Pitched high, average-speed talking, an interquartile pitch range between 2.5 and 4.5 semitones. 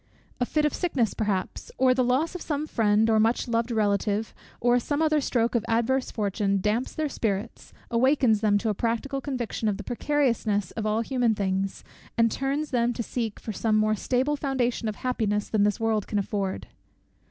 Yes: high, 230 Hz; average, 190 wpm; average, 3.6 semitones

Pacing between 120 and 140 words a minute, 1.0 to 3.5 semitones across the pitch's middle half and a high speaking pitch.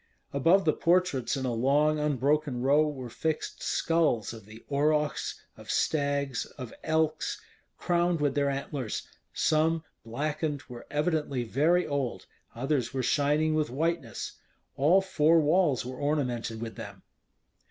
No: slow, 135 wpm; average, 3.2 semitones; medium, 145 Hz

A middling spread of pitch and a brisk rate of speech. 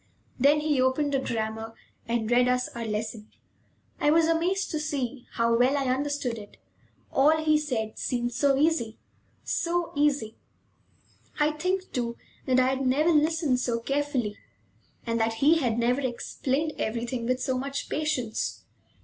No: average, 4.2 semitones; average, 155 wpm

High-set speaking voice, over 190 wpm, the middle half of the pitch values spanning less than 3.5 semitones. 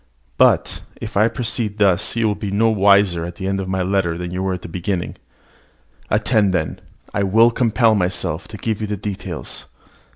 No: low, 100 Hz; average, 200 wpm; average, 2.8 semitones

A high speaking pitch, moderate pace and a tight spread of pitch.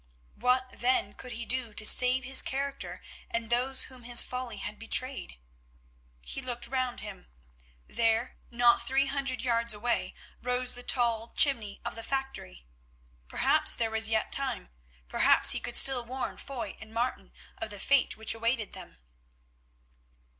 Yes: high, 245 Hz; average, 155 wpm; narrow, 2.3 semitones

